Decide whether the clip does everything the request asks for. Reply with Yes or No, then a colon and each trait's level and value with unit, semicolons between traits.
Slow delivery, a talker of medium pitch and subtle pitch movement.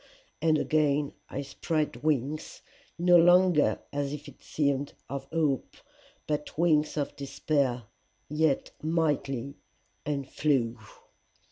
Yes: slow, 105 wpm; medium, 150 Hz; narrow, 2.1 semitones